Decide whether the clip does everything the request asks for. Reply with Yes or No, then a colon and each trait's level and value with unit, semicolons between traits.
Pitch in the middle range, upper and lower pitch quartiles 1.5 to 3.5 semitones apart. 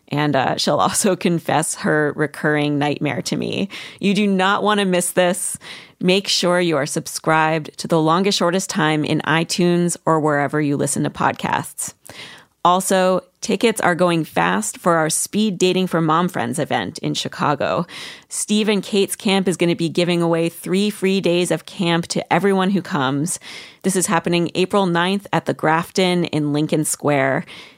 Yes: medium, 175 Hz; average, 3.2 semitones